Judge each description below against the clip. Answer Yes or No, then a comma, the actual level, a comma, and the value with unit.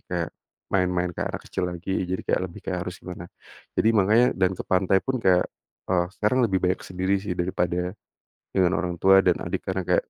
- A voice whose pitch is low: Yes, very low, 90 Hz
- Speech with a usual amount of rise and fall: No, narrow, 1.3 semitones